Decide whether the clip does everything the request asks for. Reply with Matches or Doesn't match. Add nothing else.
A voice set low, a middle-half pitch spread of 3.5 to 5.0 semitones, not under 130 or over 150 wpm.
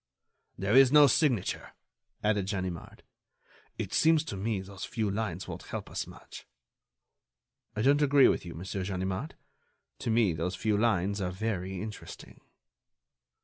Matches